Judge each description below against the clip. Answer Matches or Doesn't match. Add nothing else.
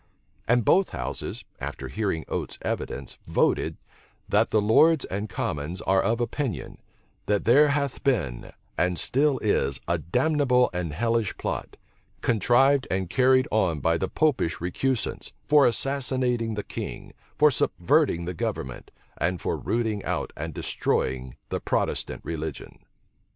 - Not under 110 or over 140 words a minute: Matches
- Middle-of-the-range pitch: Doesn't match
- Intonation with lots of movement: Matches